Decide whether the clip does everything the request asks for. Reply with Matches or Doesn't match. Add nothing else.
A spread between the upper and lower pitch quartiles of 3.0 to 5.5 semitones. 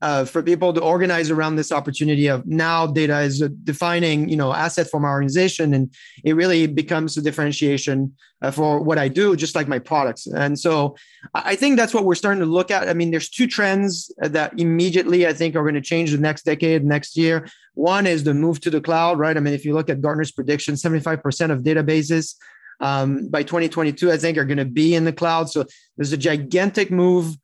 Doesn't match